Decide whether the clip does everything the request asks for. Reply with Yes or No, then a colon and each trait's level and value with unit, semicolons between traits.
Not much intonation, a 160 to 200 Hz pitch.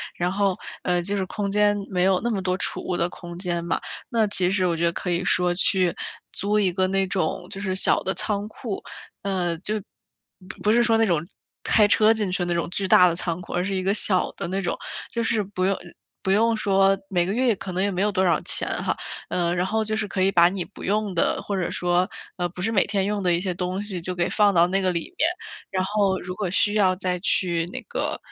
Yes: narrow, 2.3 semitones; high, 190 Hz